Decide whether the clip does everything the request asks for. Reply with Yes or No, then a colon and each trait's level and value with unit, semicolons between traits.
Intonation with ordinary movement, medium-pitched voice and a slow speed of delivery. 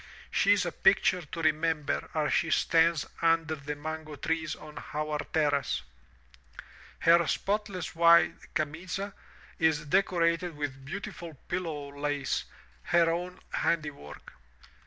No: narrow, 2.2 semitones; medium, 160 Hz; slow, 115 wpm